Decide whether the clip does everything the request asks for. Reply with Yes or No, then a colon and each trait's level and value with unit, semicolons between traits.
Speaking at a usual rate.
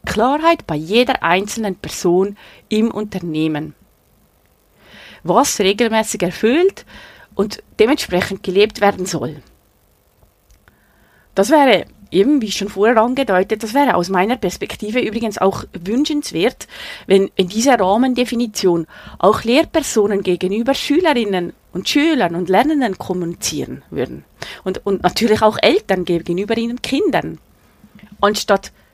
No: slow, 110 wpm